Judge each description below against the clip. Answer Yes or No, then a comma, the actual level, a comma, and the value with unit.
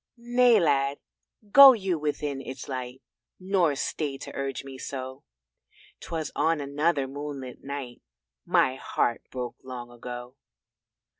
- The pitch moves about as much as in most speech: Yes, average, 3.6 semitones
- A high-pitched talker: No, medium, 140 Hz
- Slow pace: Yes, slow, 125 wpm